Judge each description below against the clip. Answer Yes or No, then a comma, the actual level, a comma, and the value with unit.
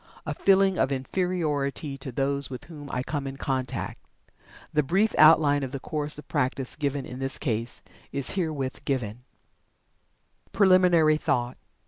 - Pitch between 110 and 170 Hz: Yes, medium, 140 Hz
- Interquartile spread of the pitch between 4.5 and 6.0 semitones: No, average, 3.1 semitones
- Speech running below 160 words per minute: Yes, average, 145 wpm